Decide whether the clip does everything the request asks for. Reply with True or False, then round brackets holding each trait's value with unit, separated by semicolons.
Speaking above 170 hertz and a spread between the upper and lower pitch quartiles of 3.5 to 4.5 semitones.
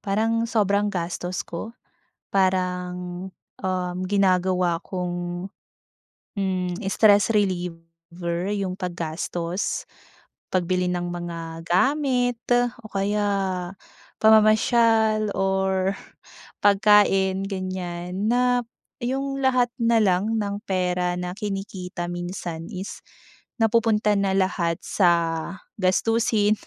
False (190 Hz; 3.1 semitones)